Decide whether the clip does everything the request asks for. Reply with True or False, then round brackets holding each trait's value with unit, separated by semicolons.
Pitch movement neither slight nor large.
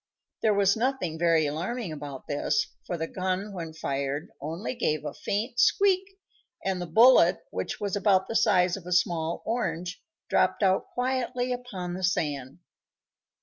False (5.8 semitones)